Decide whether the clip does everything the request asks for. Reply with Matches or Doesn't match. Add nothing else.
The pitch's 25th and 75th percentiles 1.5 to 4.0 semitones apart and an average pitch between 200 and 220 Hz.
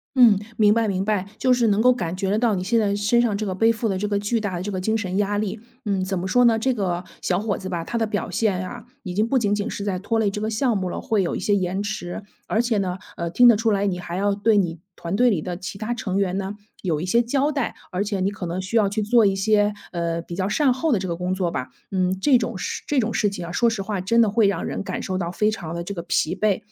Matches